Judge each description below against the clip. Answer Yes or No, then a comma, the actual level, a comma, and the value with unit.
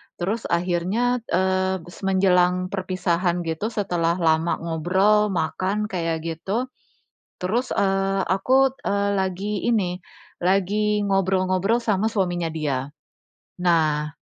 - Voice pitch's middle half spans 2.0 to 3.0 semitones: Yes, average, 2.7 semitones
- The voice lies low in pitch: No, medium, 185 Hz